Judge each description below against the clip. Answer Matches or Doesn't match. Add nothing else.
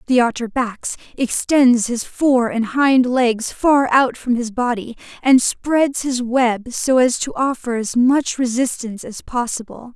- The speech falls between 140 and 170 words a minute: Matches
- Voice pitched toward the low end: Doesn't match